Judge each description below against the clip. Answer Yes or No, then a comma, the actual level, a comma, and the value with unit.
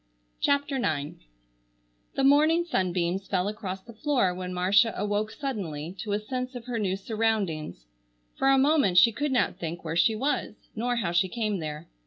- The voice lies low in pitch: No, high, 210 Hz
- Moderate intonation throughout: No, wide, 5.8 semitones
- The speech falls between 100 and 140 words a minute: No, average, 175 wpm